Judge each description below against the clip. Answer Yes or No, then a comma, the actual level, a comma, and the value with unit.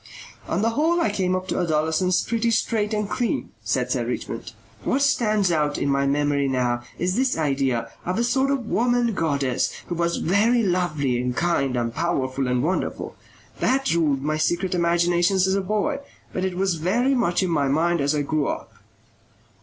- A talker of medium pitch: Yes, medium, 175 Hz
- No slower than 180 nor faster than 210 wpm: Yes, average, 185 wpm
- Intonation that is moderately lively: No, wide, 6.6 semitones